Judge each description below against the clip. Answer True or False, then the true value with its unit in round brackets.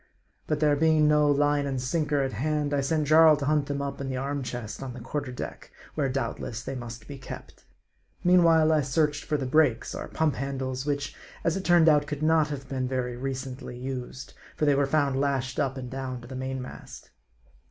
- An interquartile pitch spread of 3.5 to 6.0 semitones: False (2.5 semitones)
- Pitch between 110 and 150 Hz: True (140 Hz)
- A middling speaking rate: False (220 wpm)